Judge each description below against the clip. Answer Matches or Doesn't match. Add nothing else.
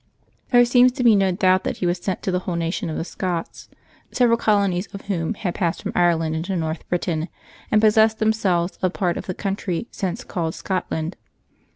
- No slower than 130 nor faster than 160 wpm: Doesn't match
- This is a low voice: Doesn't match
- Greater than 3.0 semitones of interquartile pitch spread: Matches